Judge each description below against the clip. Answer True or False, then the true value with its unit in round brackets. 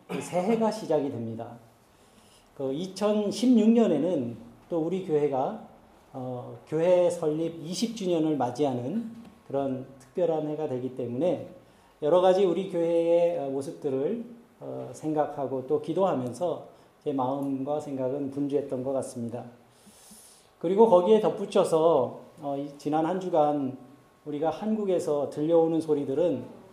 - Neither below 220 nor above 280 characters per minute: True (260 characters per minute)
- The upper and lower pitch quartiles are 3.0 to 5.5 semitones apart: True (5.1 semitones)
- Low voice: False (155 Hz)